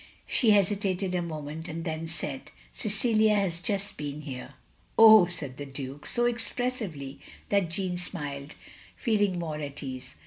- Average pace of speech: Yes, average, 145 wpm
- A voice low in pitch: No, medium, 175 Hz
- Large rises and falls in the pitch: Yes, wide, 5.7 semitones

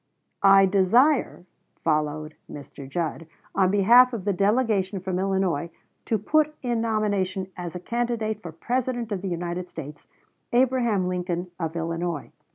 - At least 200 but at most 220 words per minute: No, average, 140 wpm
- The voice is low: No, high, 190 Hz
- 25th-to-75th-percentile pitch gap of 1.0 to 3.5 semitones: No, average, 4.6 semitones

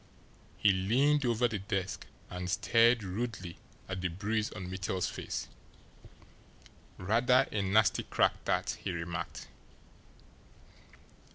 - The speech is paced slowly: Yes, slow, 110 wpm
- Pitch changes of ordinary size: Yes, average, 3.9 semitones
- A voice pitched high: No, low, 100 Hz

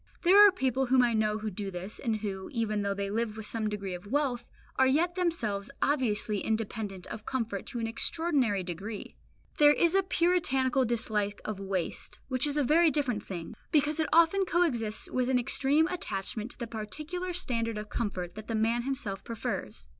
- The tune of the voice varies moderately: No, wide, 5.8 semitones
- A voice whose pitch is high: Yes, high, 230 Hz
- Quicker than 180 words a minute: Yes, average, 190 wpm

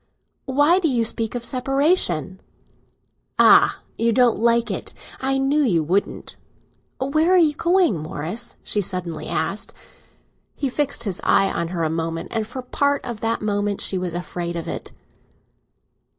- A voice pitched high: Yes, high, 230 Hz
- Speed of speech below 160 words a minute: No, average, 165 wpm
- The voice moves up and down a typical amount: No, wide, 7.1 semitones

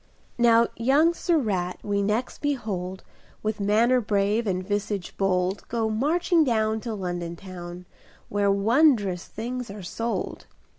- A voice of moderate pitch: No, high, 210 Hz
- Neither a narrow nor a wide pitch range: Yes, average, 3.7 semitones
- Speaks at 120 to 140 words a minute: Yes, slow, 135 wpm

